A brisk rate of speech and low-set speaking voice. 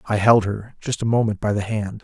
Yes: fast, 265 wpm; low, 110 Hz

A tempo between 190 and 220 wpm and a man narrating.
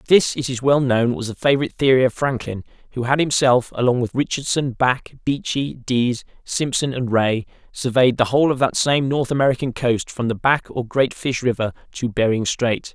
Yes: average, 195 wpm; male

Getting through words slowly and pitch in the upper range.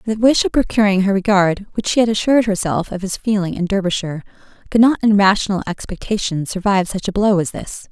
No: fast, 205 wpm; high, 200 Hz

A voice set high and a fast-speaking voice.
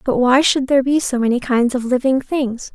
Yes: very high, 255 Hz; fast, 240 wpm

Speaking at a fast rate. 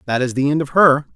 Yes: fast, 310 wpm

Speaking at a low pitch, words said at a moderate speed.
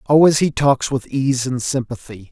Yes: low, 130 Hz; average, 180 wpm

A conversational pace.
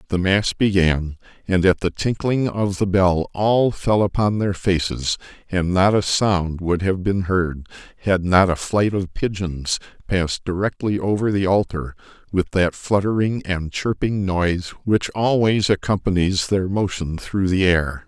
Yes: average, 160 wpm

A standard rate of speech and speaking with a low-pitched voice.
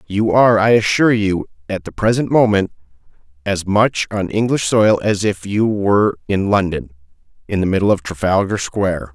Yes: average, 170 wpm; low, 100 Hz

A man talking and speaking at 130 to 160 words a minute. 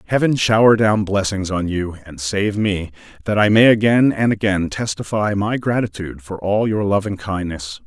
No: male; average, 185 wpm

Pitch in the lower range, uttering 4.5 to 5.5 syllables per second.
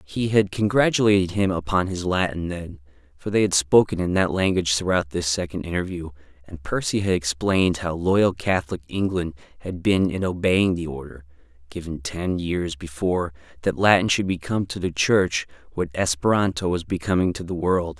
Yes: very low, 90 Hz; 5.3 syllables/s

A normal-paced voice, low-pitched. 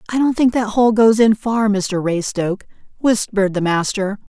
No: average, 180 wpm; high, 210 Hz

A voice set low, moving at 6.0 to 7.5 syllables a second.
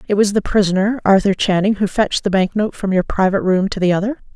No: high, 200 Hz; 6.5 syllables/s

